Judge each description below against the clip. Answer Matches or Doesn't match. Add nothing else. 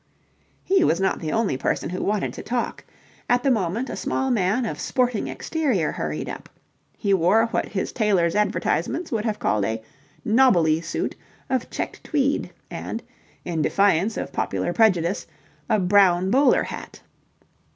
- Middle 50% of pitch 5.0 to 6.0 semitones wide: Matches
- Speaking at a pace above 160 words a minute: Doesn't match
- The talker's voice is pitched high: Matches